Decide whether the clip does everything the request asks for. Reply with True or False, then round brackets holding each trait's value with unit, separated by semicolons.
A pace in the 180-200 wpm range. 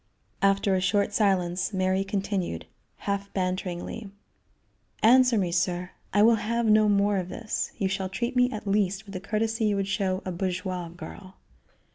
False (165 wpm)